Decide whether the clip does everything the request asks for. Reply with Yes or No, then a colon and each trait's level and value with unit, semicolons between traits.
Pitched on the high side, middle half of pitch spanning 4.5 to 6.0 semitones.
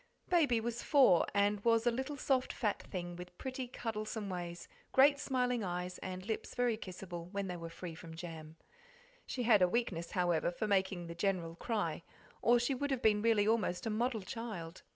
Yes: high, 205 Hz; average, 5.1 semitones